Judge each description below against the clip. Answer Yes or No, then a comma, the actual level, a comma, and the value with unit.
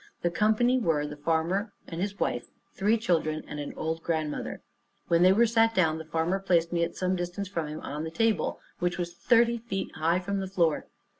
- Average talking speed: No, fast, 210 wpm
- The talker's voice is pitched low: No, medium, 175 Hz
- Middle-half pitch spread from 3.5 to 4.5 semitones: Yes, average, 3.8 semitones